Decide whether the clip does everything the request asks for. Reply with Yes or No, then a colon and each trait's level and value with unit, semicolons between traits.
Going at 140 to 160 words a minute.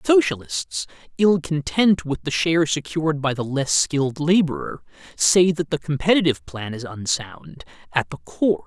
Yes: average, 150 wpm